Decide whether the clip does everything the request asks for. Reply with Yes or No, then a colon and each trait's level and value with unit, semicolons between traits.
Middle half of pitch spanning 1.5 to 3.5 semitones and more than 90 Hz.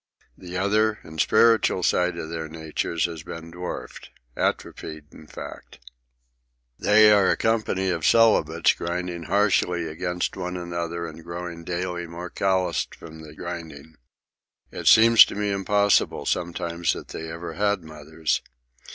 No: average, 2.7 semitones; very low, 85 Hz